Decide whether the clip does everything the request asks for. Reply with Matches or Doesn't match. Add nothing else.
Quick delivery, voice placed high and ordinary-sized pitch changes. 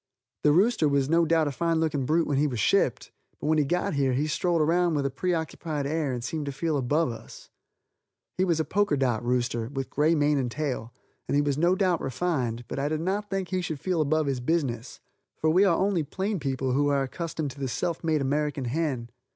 Doesn't match